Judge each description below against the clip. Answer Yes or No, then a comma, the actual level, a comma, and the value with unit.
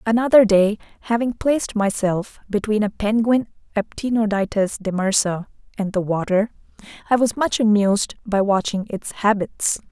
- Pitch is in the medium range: No, high, 210 Hz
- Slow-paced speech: Yes, slow, 125 wpm